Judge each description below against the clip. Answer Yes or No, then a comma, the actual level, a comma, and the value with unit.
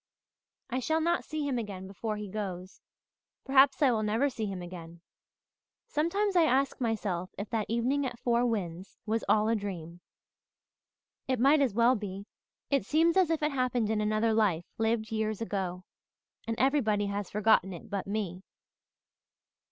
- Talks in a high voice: Yes, high, 220 Hz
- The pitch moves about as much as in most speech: Yes, average, 4.7 semitones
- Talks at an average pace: Yes, average, 165 wpm